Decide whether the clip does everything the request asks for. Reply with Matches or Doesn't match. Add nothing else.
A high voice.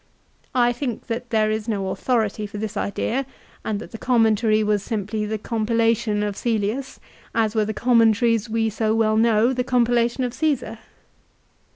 Matches